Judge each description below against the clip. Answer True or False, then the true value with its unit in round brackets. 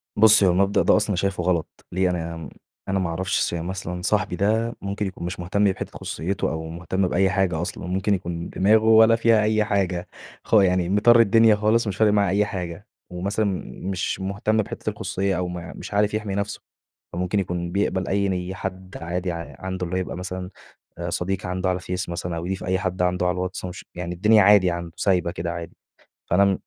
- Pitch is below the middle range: True (95 Hz)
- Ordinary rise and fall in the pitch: False (2.2 semitones)